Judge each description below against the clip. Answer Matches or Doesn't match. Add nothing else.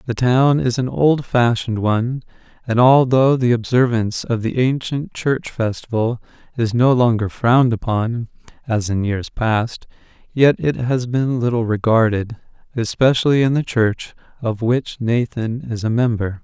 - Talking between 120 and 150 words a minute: Matches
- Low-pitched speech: Matches